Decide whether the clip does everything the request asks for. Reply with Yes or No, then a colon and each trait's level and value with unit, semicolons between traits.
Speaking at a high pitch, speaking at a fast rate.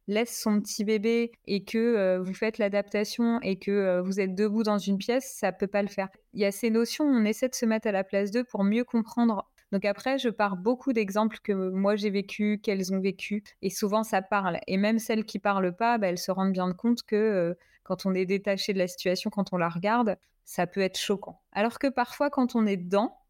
Yes: high, 210 Hz; fast, 240 wpm